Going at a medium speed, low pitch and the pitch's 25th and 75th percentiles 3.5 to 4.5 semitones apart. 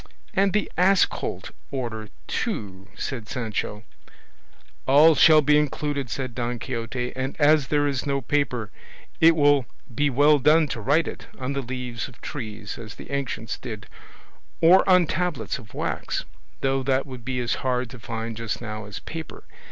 Yes: average, 165 wpm; low, 130 Hz; average, 4.1 semitones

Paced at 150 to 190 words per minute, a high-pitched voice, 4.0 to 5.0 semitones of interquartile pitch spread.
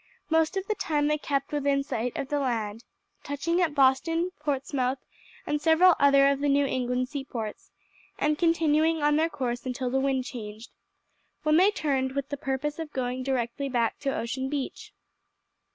No: average, 170 wpm; very high, 275 Hz; average, 2.7 semitones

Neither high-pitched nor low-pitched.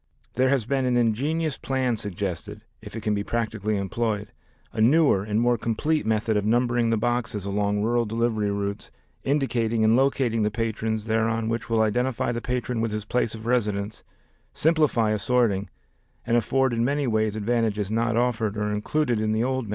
No: low, 115 Hz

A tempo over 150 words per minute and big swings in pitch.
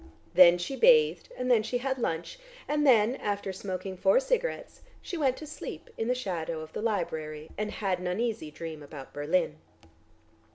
Yes: average, 175 wpm; wide, 7.8 semitones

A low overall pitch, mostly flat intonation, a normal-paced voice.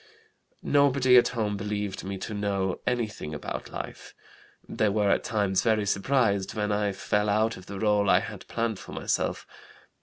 Yes: low, 105 Hz; narrow, 2.0 semitones; average, 170 wpm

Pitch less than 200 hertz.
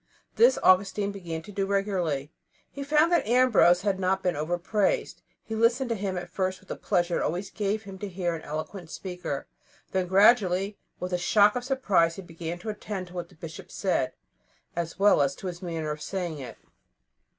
Yes: medium, 185 Hz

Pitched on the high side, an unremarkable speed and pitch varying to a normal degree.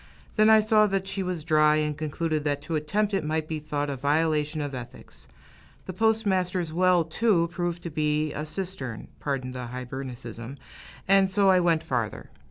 No: medium, 155 Hz; average, 175 wpm; average, 4.3 semitones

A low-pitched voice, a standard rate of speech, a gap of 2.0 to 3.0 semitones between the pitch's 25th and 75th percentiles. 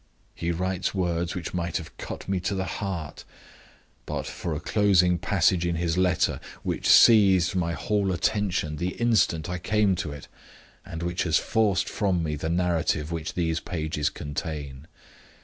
Yes: very low, 90 Hz; average, 165 wpm; average, 2.7 semitones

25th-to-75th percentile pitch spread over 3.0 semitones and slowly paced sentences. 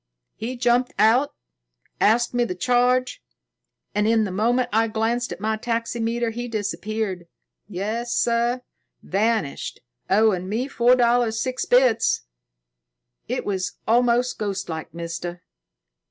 No: average, 2.7 semitones; slow, 125 wpm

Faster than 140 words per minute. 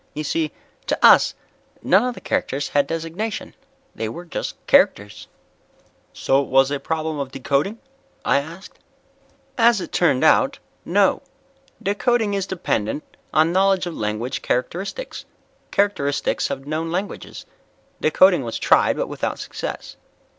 No: slow, 135 wpm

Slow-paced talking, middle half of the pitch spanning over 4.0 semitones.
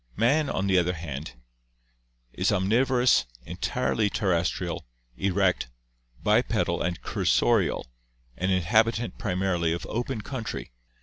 Yes: slow, 110 wpm; average, 4.6 semitones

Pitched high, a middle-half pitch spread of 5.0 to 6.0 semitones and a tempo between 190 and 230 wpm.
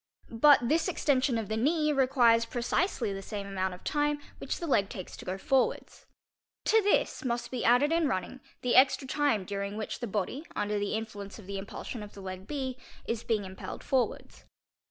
Yes: high, 235 Hz; wide, 5.4 semitones; average, 195 wpm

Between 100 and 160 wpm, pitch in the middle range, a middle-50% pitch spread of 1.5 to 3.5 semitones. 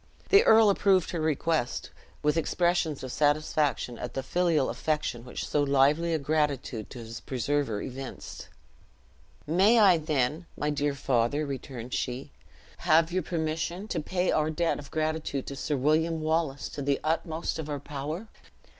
Yes: average, 155 wpm; medium, 150 Hz; average, 3.2 semitones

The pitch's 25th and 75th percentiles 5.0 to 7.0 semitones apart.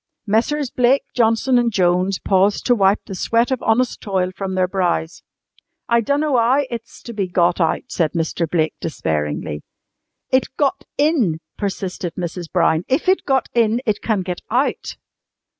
Yes: wide, 5.5 semitones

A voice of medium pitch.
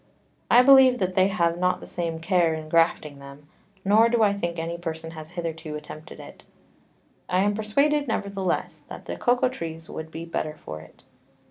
Yes: medium, 170 Hz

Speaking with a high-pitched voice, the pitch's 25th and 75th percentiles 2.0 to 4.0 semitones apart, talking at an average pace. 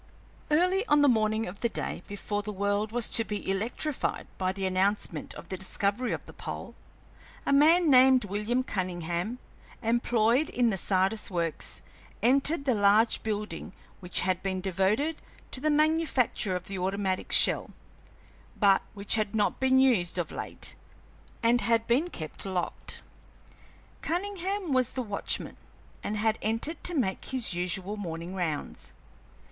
No: high, 215 Hz; average, 5.2 semitones; average, 150 wpm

